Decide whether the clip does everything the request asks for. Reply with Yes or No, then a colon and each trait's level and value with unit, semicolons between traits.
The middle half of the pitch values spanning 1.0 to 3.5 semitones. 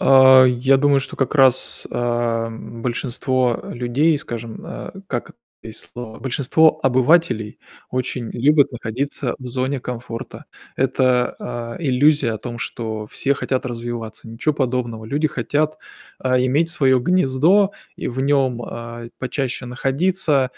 Yes: average, 2.8 semitones